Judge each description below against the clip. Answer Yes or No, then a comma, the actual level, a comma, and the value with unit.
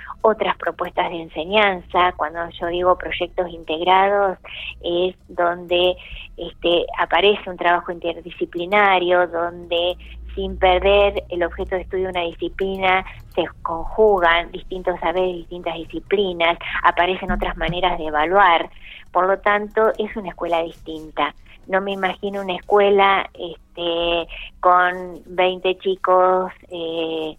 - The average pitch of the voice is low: No, medium, 180 Hz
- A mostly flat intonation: Yes, narrow, 1.8 semitones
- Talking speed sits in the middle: No, slow, 120 wpm